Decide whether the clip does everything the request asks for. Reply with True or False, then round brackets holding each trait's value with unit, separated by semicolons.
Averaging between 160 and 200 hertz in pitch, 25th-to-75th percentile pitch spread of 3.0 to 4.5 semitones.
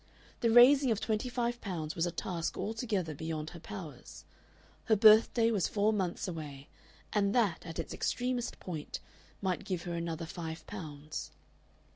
False (185 Hz; 5.4 semitones)